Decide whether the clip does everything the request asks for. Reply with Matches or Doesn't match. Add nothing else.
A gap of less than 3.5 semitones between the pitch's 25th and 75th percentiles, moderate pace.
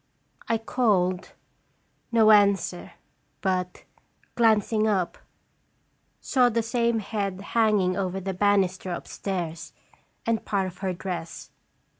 Doesn't match